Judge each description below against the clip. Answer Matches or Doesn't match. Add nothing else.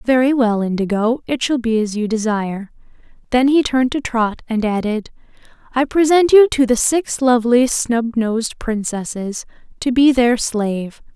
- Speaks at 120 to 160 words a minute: Matches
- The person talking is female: Matches